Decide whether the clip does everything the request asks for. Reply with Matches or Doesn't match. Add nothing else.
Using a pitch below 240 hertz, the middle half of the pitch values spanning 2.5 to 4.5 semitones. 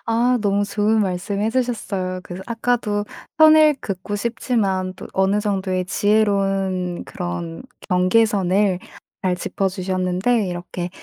Matches